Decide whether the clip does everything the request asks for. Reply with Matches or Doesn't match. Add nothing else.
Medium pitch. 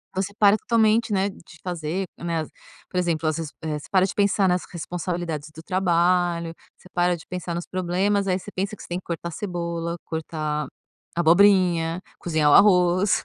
Matches